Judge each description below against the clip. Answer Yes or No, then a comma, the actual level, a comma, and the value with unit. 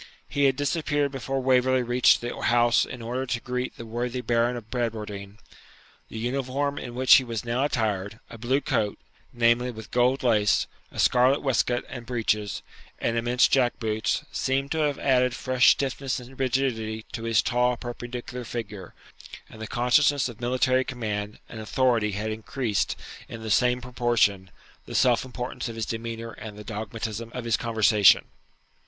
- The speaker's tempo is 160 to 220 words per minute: Yes, average, 165 wpm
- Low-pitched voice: Yes, low, 120 Hz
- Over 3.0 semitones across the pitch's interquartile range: No, narrow, 2.5 semitones